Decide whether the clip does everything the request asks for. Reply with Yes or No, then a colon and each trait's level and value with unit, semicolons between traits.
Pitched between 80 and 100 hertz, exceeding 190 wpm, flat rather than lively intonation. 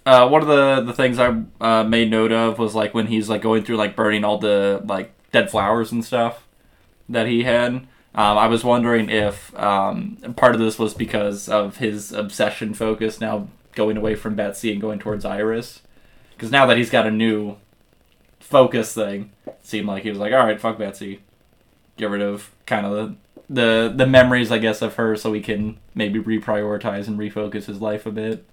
No: low, 110 Hz; fast, 205 wpm; narrow, 1.6 semitones